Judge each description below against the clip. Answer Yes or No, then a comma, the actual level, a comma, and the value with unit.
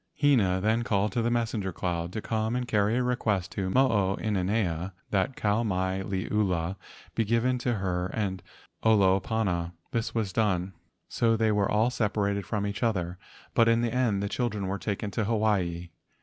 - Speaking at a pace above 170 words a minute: Yes, average, 180 wpm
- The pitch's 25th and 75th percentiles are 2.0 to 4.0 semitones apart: Yes, average, 3.3 semitones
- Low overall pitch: Yes, low, 105 Hz